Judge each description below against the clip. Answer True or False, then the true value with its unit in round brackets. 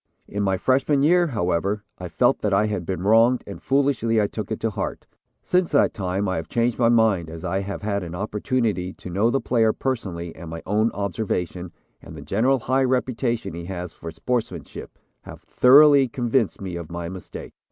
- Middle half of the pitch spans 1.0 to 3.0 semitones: False (5.2 semitones)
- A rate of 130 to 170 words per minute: False (195 wpm)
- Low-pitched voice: True (105 Hz)